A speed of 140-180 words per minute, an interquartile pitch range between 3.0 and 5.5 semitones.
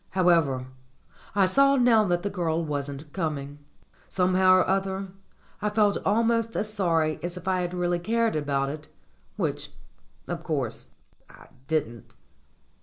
Yes: average, 145 wpm; average, 4.6 semitones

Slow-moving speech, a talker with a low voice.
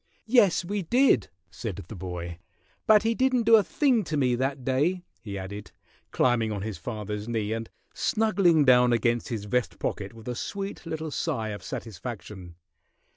No: average, 170 wpm; low, 125 Hz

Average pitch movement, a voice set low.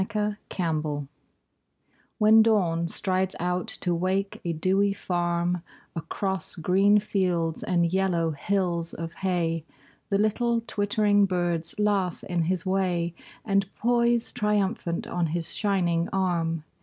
No: average, 3.0 semitones; medium, 185 Hz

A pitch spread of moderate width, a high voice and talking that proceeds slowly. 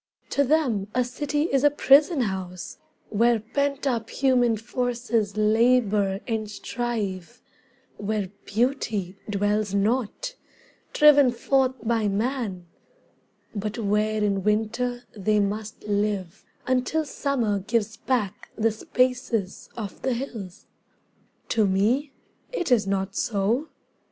Yes: average, 3.7 semitones; high, 225 Hz; slow, 115 wpm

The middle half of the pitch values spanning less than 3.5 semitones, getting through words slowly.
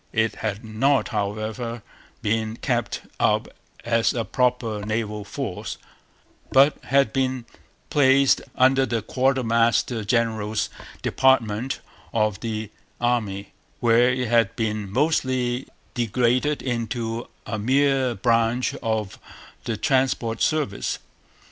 Yes: average, 2.9 semitones; slow, 105 wpm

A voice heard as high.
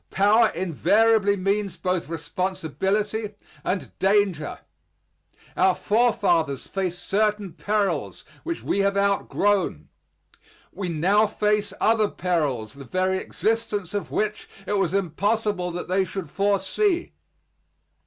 Yes: high, 195 Hz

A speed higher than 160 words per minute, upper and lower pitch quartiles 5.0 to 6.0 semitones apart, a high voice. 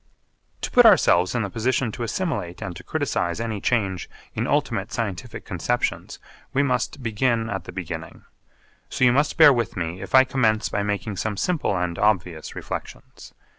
No: average, 170 wpm; wide, 5.4 semitones; low, 110 Hz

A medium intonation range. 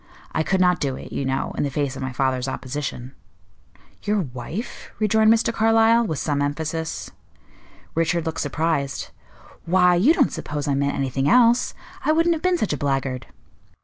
No: wide, 8.0 semitones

